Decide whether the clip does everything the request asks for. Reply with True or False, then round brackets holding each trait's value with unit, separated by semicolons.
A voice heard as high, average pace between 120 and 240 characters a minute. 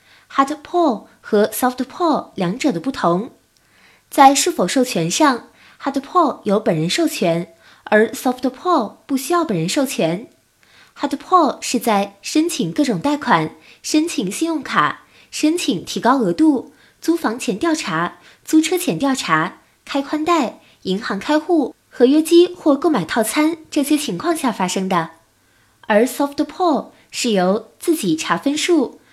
False (275 Hz; 260 characters per minute)